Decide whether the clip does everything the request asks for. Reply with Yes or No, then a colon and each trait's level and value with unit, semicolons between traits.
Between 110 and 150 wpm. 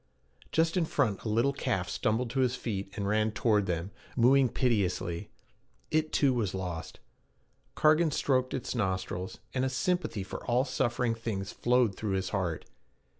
No: average, 160 wpm